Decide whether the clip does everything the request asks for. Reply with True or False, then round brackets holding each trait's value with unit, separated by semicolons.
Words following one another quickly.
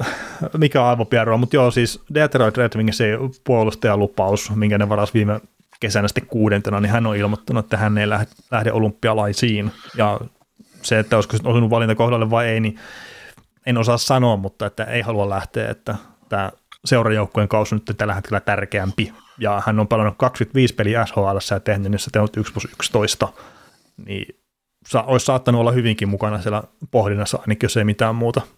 True (175 wpm)